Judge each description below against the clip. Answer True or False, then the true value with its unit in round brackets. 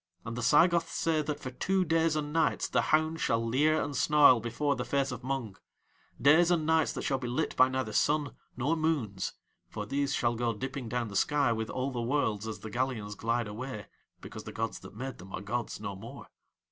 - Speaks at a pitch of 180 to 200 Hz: False (130 Hz)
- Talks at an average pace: False (215 wpm)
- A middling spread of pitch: True (4.7 semitones)